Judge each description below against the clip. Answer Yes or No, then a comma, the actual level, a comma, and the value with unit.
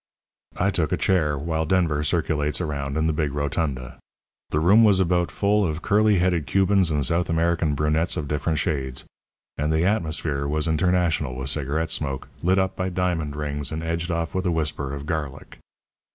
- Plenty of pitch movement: No, average, 3.2 semitones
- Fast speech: No, average, 180 wpm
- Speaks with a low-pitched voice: Yes, very low, 80 Hz